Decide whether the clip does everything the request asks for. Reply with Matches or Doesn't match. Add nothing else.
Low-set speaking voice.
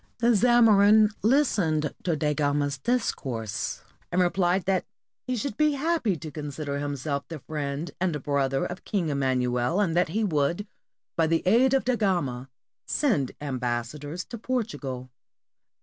Doesn't match